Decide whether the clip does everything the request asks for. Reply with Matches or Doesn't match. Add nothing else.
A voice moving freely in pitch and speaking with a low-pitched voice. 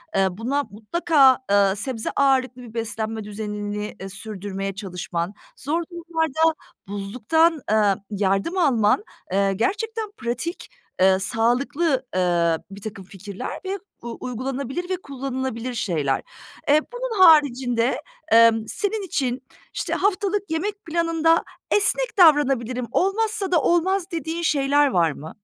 Doesn't match